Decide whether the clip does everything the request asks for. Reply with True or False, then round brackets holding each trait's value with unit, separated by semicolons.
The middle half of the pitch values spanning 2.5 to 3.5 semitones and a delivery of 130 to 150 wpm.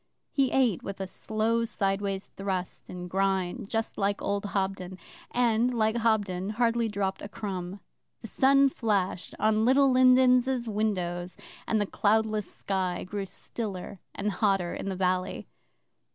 True (3.1 semitones; 140 wpm)